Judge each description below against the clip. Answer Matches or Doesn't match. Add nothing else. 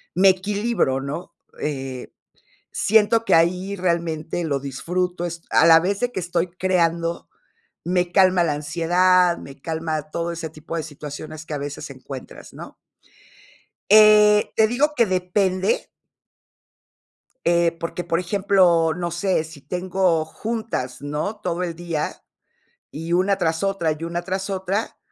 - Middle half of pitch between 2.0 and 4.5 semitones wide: Matches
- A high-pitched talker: Doesn't match